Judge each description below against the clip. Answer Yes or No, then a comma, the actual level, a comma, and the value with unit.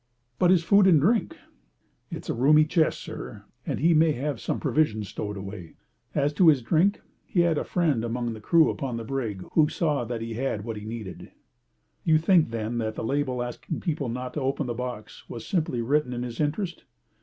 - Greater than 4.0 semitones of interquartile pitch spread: Yes, wide, 5.4 semitones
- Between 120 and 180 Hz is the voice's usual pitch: Yes, low, 135 Hz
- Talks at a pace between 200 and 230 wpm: Yes, fast, 205 wpm